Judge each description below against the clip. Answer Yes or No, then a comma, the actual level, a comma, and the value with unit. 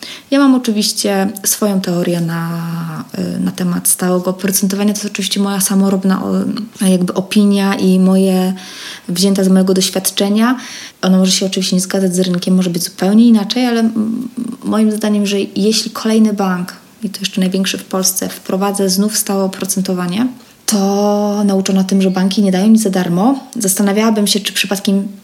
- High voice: Yes, high, 195 Hz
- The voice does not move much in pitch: Yes, narrow, 2.0 semitones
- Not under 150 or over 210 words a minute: Yes, average, 155 wpm